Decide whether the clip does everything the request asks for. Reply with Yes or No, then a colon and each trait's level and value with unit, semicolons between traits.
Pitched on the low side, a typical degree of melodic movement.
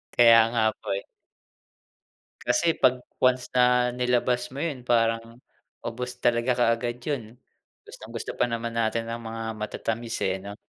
No: low, 120 Hz; narrow, 1.4 semitones